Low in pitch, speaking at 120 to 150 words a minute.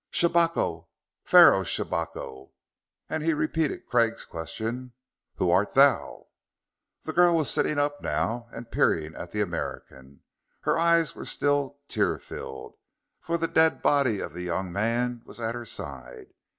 Yes: low, 120 Hz; average, 145 wpm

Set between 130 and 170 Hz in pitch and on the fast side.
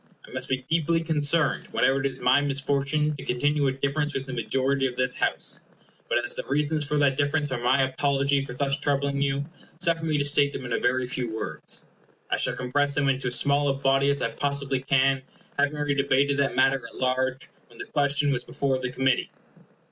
Yes: medium, 140 Hz; fast, 215 wpm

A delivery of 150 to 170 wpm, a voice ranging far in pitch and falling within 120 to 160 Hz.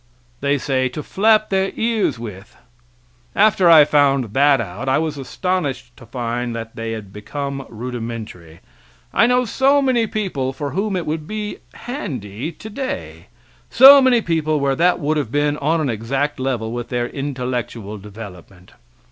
Yes: average, 155 wpm; wide, 7.4 semitones; medium, 140 Hz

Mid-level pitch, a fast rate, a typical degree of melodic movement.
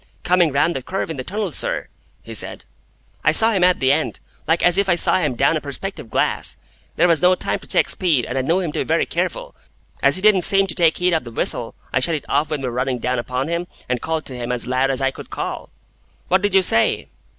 No: medium, 160 Hz; fast, 260 wpm; wide, 5.7 semitones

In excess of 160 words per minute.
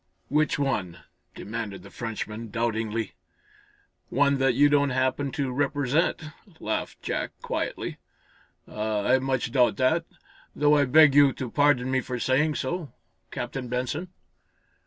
No: slow, 135 wpm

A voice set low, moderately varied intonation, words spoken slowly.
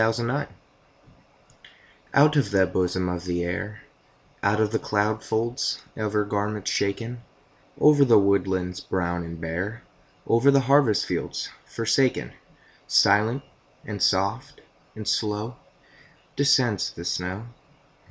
Yes: low, 105 Hz; average, 3.9 semitones; slow, 125 wpm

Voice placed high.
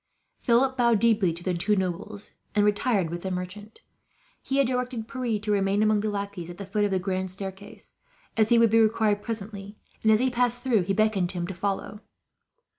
Yes: high, 205 Hz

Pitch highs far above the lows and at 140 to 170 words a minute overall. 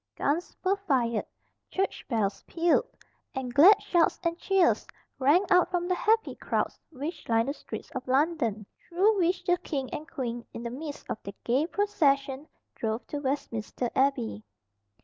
Yes: wide, 6.4 semitones; average, 160 wpm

